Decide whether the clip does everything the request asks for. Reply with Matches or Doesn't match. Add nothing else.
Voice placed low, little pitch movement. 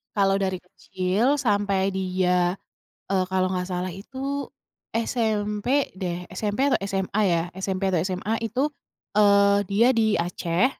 Doesn't match